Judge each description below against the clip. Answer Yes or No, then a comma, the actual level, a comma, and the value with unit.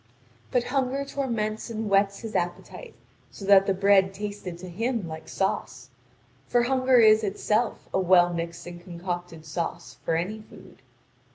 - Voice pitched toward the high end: Yes, high, 200 Hz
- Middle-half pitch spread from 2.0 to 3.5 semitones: No, average, 4.4 semitones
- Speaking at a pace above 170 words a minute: No, average, 155 wpm